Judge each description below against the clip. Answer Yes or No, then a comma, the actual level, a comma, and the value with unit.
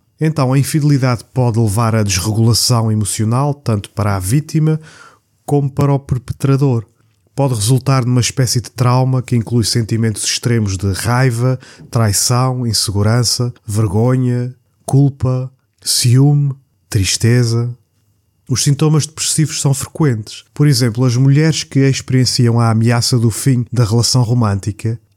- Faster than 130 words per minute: No, average, 125 wpm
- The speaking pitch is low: Yes, low, 125 Hz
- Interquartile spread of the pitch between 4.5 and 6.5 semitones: No, average, 3.1 semitones